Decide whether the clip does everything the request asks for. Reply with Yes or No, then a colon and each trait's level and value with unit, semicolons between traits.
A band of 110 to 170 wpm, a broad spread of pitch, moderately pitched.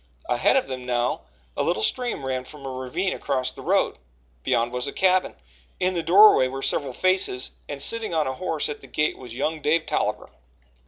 No: average, 200 wpm; wide, 6.0 semitones; medium, 145 Hz